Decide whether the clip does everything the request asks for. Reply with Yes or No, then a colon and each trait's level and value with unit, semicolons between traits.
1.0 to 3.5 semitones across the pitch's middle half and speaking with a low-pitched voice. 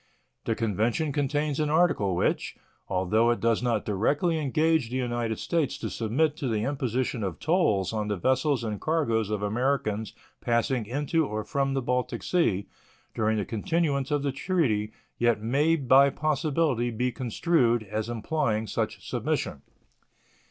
No: average, 5.1 semitones; low, 125 Hz